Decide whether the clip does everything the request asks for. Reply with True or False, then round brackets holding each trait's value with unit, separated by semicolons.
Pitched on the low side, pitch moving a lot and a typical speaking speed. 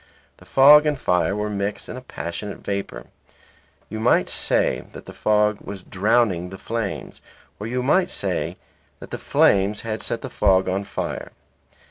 False (105 Hz; 3.3 semitones; 165 wpm)